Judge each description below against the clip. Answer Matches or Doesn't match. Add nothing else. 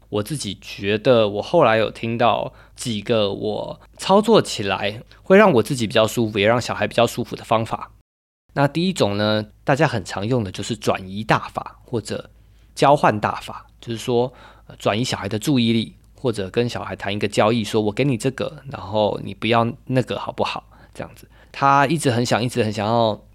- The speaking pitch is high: Doesn't match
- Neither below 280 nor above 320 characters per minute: Matches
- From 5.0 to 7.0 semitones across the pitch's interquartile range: Doesn't match